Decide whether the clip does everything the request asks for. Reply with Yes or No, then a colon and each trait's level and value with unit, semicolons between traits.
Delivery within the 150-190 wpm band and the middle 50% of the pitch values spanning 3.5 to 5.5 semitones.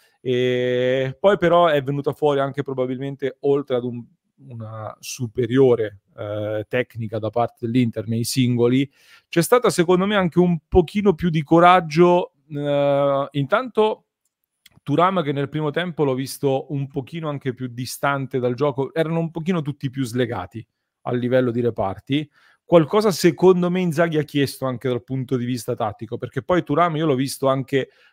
Yes: average, 160 wpm; average, 4.8 semitones